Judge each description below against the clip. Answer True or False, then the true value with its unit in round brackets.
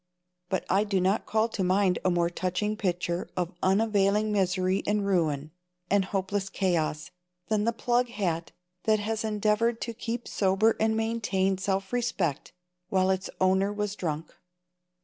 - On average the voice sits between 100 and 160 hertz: False (195 Hz)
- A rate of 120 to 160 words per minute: True (150 wpm)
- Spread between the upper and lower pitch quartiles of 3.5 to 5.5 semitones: False (2.6 semitones)